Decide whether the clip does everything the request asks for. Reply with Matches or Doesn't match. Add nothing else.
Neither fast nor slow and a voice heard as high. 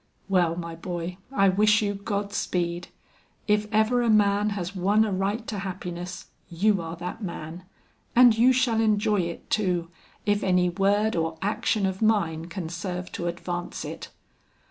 Matches